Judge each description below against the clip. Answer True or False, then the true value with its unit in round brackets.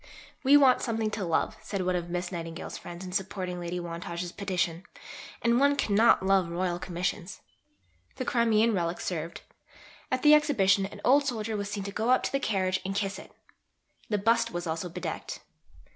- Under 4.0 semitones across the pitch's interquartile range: False (4.3 semitones)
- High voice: True (195 Hz)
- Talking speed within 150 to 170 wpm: False (180 wpm)